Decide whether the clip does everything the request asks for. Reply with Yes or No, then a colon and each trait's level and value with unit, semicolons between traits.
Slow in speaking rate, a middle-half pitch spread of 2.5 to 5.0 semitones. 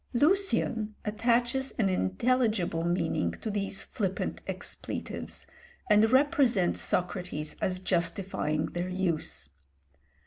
No: slow, 95 wpm; wide, 5.4 semitones